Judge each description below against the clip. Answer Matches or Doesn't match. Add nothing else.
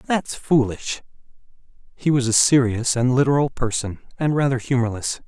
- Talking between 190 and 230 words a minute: Doesn't match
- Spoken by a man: Matches